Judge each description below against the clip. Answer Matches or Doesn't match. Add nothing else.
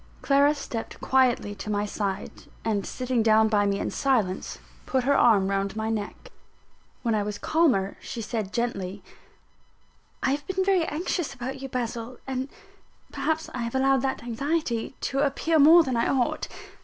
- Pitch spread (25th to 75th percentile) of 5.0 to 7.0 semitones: Doesn't match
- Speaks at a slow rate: Doesn't match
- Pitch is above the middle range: Matches